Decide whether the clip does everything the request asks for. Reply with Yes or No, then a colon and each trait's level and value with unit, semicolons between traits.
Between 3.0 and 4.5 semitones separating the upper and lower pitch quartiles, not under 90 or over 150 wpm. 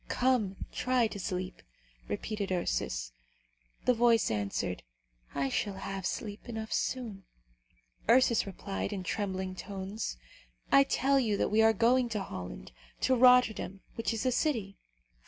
Yes: average, 4.1 semitones; slow, 135 wpm